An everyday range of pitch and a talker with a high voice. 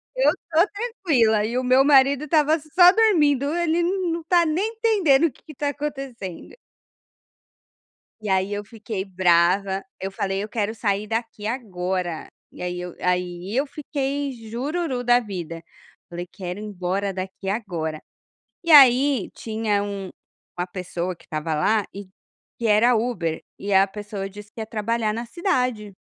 No: wide, 6.7 semitones; high, 220 Hz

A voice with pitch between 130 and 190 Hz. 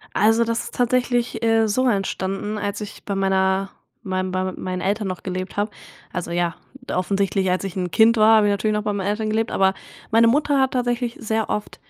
No: high, 205 Hz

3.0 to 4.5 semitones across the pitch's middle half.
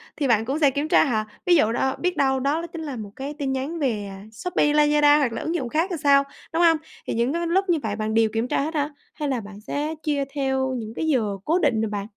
No: average, 5.2 semitones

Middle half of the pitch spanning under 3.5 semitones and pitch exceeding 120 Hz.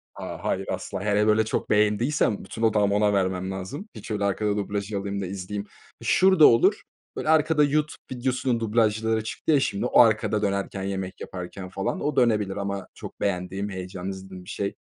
No: average, 2.8 semitones; low, 105 Hz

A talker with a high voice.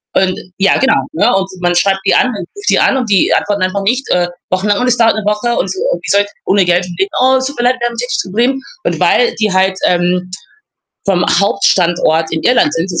Yes: high, 200 Hz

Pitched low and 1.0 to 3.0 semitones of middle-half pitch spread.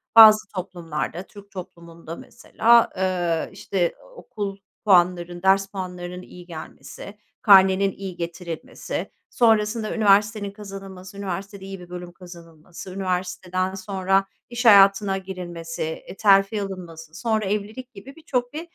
No: high, 190 Hz; narrow, 2.4 semitones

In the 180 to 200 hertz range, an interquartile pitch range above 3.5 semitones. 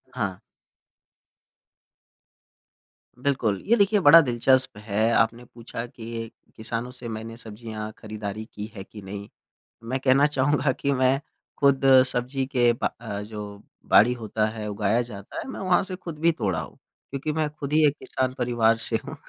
No: low, 120 Hz; average, 4.2 semitones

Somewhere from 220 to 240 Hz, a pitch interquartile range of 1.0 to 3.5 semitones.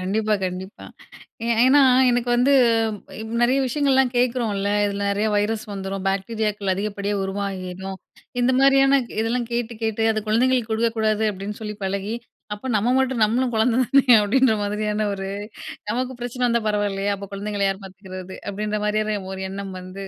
No: high, 210 Hz; average, 3.2 semitones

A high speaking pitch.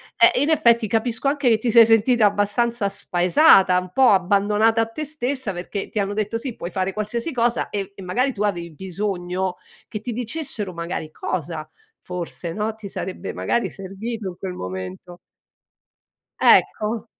Yes: high, 210 Hz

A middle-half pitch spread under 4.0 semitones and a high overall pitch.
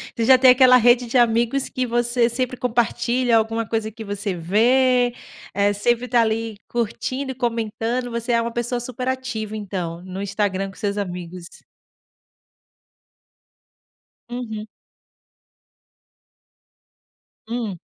Yes: average, 2.8 semitones; high, 230 Hz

